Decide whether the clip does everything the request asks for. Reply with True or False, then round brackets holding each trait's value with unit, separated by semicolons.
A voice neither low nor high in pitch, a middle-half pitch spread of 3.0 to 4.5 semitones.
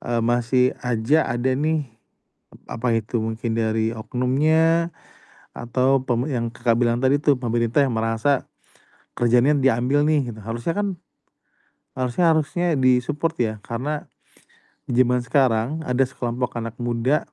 False (125 Hz; 3.3 semitones)